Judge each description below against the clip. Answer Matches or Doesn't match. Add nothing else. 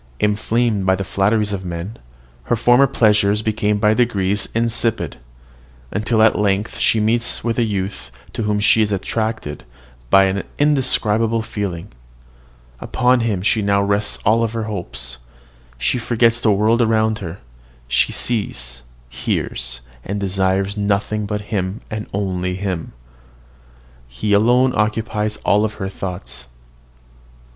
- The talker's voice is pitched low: Matches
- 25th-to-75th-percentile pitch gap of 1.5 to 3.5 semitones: Matches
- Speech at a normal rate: Doesn't match